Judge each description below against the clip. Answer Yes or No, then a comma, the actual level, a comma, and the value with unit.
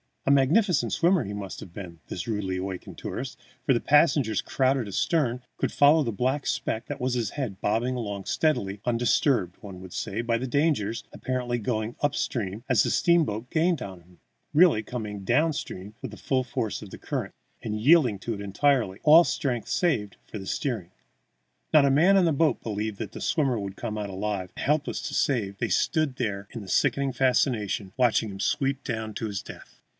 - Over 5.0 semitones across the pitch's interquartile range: Yes, wide, 5.5 semitones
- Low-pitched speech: Yes, low, 120 Hz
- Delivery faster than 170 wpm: Yes, average, 190 wpm